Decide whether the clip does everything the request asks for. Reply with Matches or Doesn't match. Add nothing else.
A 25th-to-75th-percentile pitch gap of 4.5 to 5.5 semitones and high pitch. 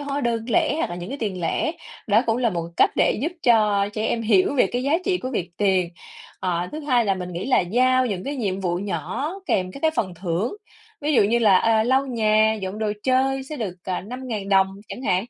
Matches